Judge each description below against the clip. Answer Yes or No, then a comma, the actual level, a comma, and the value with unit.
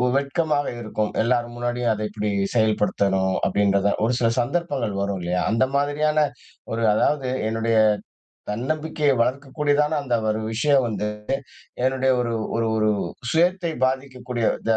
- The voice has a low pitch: Yes, low, 120 Hz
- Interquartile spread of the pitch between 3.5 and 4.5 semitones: No, average, 4.9 semitones